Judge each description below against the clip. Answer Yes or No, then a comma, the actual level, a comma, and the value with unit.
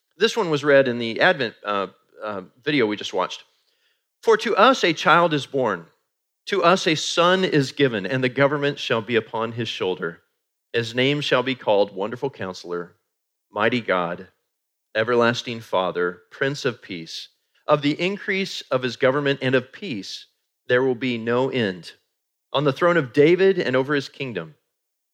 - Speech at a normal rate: Yes, average, 170 wpm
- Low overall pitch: Yes, low, 130 Hz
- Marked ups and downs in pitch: No, average, 4.4 semitones